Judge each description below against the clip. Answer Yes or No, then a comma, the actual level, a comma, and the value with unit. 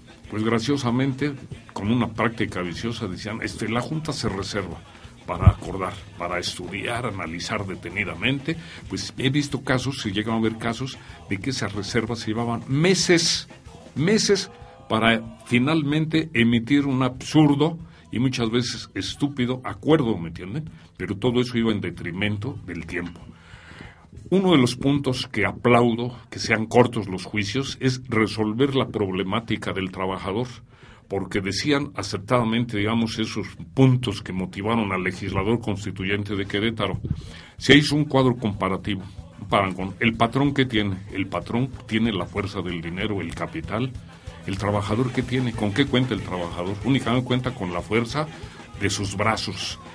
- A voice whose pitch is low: Yes, low, 110 Hz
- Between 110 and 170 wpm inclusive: Yes, average, 145 wpm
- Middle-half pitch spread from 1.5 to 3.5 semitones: No, average, 4.3 semitones